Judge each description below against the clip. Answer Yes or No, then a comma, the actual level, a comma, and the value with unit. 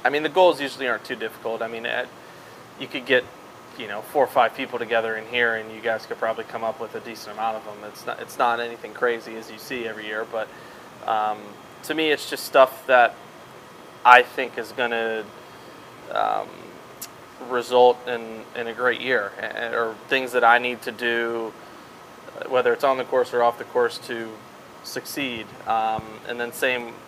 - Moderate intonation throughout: No, narrow, 1.8 semitones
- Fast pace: No, average, 195 wpm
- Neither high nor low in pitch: No, low, 115 Hz